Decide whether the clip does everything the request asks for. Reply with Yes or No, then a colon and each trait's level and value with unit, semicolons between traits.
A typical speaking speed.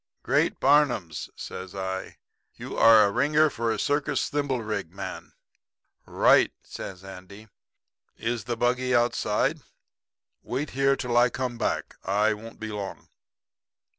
No: slow, 125 wpm